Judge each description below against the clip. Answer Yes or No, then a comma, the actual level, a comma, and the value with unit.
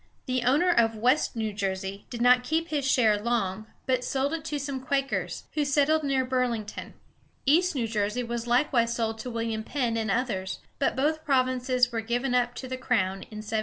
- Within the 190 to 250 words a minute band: Yes, average, 200 wpm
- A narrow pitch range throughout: No, average, 3.4 semitones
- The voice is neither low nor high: No, very high, 250 Hz